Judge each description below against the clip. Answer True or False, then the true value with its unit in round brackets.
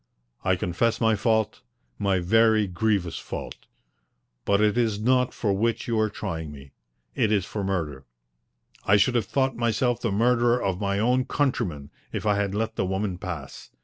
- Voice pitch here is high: False (105 Hz)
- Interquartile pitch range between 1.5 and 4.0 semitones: True (3.5 semitones)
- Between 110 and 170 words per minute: False (180 wpm)